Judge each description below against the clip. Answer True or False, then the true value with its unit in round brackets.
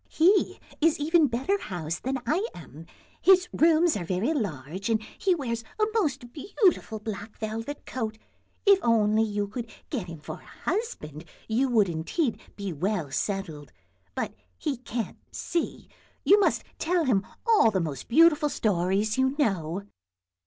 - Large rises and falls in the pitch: True (8.1 semitones)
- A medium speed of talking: True (150 wpm)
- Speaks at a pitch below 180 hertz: False (230 Hz)